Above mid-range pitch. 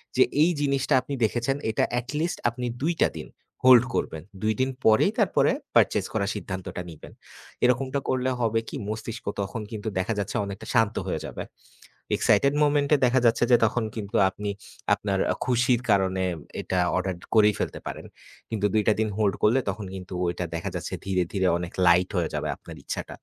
No: low, 110 Hz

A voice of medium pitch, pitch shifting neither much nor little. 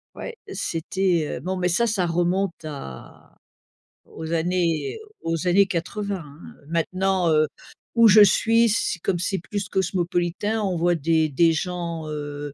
Yes: medium, 175 Hz; average, 3.0 semitones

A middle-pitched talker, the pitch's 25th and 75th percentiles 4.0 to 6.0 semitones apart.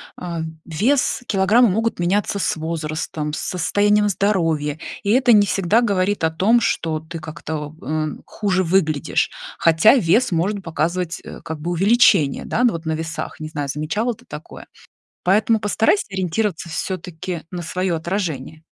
Yes: medium, 180 Hz; average, 4.4 semitones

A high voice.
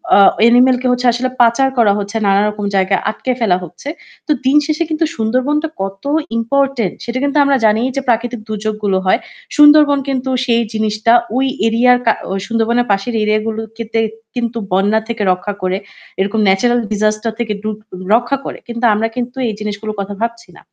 Yes: high, 230 Hz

